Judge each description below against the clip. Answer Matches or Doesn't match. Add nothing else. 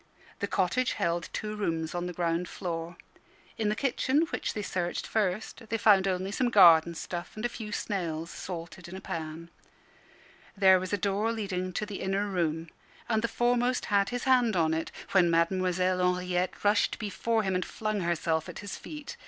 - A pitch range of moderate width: Matches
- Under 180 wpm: Doesn't match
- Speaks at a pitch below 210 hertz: Matches